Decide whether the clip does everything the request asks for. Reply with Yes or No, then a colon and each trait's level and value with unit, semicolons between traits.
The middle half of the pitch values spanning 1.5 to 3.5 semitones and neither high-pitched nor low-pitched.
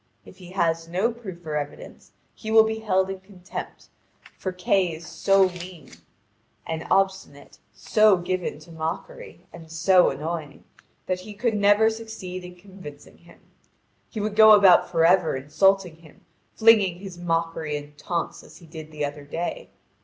Yes: average, 3.2 semitones; medium, 180 Hz